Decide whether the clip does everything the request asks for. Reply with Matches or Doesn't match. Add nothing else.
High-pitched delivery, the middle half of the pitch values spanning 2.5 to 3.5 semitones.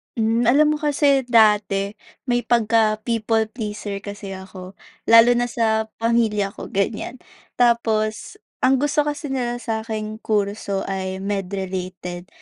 Matches